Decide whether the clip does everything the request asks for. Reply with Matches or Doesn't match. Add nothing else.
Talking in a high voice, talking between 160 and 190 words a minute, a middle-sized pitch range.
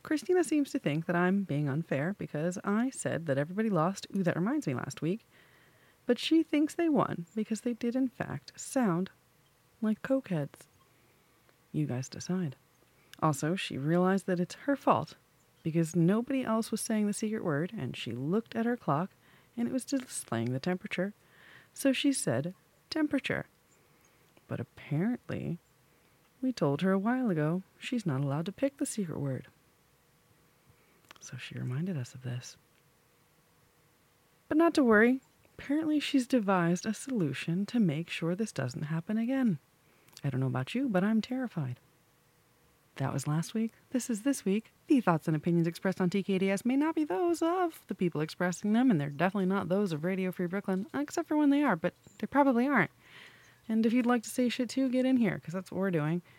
Doesn't match